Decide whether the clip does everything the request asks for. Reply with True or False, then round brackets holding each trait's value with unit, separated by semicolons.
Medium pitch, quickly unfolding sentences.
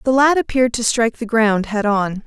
False (230 Hz; 240 wpm)